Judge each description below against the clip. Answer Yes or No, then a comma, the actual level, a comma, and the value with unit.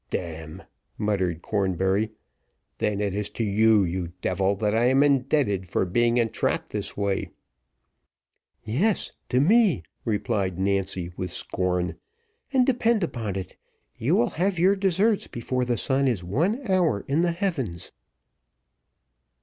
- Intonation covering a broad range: Yes, wide, 8.6 semitones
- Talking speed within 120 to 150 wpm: Yes, average, 140 wpm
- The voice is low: Yes, low, 110 Hz